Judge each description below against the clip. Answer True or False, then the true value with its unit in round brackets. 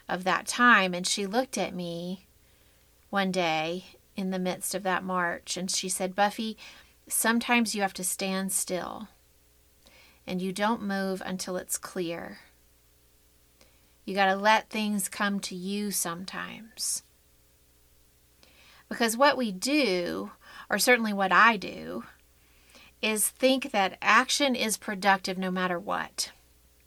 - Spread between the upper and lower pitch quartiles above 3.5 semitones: True (5.0 semitones)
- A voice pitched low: False (185 Hz)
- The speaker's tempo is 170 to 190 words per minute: False (135 wpm)